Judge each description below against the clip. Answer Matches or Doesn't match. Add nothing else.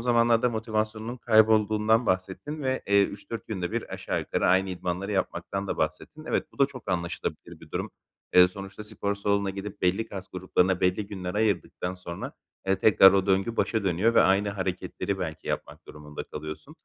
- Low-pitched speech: Matches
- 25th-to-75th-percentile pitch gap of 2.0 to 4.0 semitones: Matches